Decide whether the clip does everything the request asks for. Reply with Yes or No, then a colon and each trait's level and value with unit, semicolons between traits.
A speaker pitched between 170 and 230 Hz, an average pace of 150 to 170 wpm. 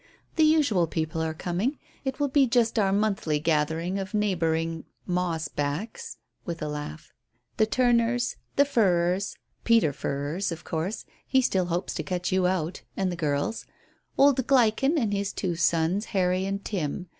Yes: medium, 185 Hz; average, 160 wpm